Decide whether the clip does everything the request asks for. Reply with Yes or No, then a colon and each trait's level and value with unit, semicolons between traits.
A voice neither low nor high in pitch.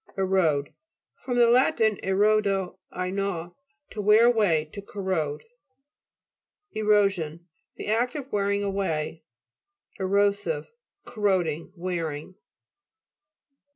No: high, 195 Hz